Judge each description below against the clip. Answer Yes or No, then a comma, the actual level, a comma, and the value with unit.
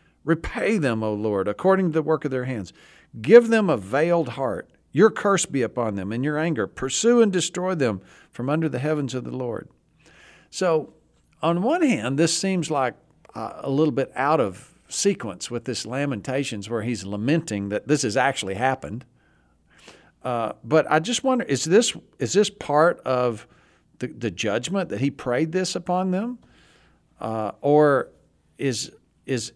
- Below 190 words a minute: Yes, average, 170 wpm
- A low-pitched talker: No, medium, 145 Hz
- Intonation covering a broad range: Yes, wide, 6.6 semitones